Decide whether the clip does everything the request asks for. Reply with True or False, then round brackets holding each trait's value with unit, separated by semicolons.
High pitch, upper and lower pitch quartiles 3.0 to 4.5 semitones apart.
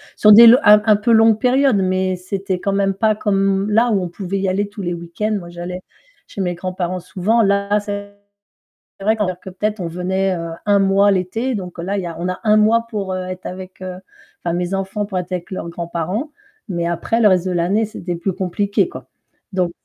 False (195 Hz; 2.4 semitones)